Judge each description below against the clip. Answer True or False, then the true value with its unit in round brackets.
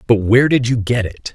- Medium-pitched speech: False (115 Hz)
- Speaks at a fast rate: True (265 wpm)